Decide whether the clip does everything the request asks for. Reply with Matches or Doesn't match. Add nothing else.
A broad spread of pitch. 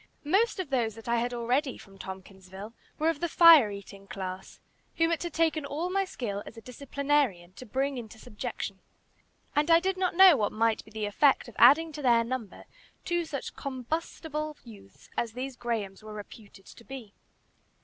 Matches